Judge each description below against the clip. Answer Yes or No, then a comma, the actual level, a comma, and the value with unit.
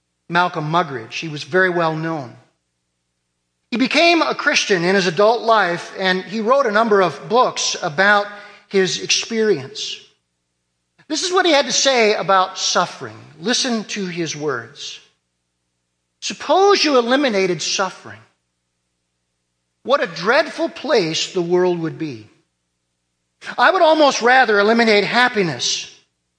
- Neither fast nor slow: No, slow, 125 wpm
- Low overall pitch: No, medium, 185 Hz